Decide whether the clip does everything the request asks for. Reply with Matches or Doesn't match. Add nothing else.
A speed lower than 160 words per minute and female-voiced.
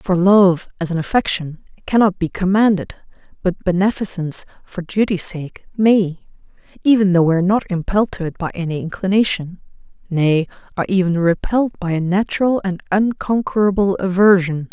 Matches